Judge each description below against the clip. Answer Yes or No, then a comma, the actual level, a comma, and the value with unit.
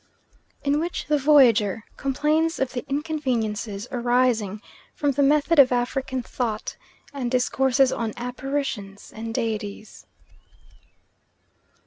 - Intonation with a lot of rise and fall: No, average, 3.9 semitones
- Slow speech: Yes, slow, 105 wpm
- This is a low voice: No, very high, 255 Hz